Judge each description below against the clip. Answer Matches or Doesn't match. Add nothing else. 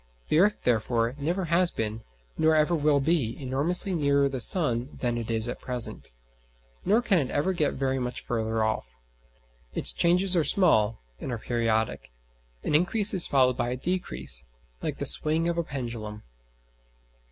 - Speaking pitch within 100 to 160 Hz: Matches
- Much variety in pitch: Matches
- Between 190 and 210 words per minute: Doesn't match